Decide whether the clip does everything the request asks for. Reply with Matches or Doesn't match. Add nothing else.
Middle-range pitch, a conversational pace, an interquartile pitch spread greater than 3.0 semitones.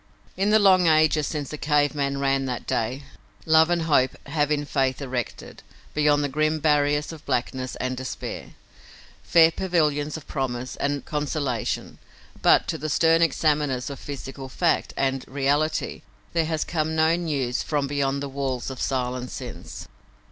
Doesn't match